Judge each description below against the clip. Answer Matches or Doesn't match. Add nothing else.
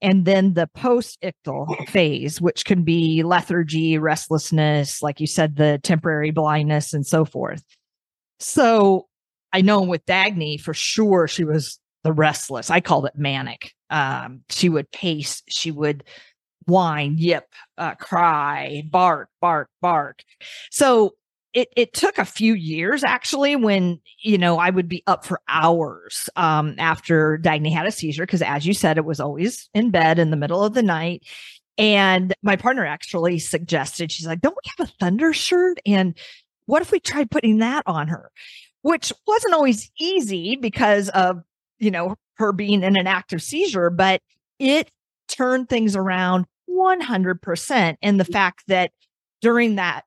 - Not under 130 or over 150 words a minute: Doesn't match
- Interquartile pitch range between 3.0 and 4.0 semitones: Doesn't match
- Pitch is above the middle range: Doesn't match